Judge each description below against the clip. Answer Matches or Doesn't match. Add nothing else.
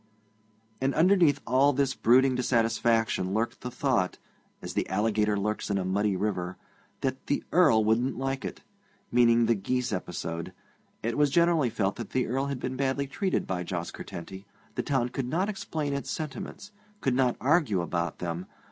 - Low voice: Matches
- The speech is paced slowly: Doesn't match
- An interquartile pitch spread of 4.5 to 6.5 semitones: Matches